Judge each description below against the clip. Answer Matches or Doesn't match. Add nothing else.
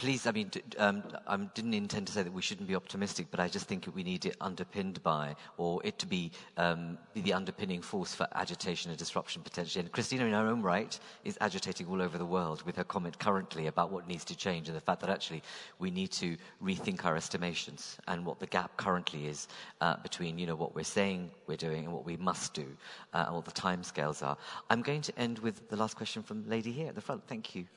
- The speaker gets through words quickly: Matches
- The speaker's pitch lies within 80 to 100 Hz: Matches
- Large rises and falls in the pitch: Matches